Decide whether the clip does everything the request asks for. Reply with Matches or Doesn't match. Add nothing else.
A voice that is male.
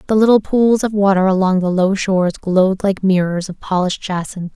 Doesn't match